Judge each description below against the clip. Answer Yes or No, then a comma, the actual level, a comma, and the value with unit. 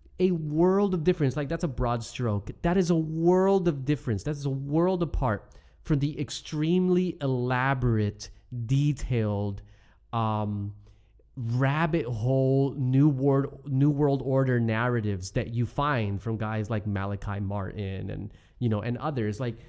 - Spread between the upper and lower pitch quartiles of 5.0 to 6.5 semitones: Yes, wide, 5.6 semitones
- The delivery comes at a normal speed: Yes, average, 145 wpm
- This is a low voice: Yes, low, 130 Hz